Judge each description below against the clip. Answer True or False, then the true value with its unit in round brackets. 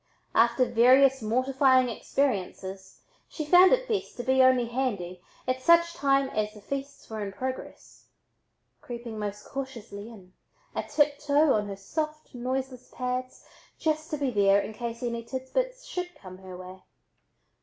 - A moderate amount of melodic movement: True (4.6 semitones)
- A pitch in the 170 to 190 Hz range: False (255 Hz)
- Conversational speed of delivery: True (150 wpm)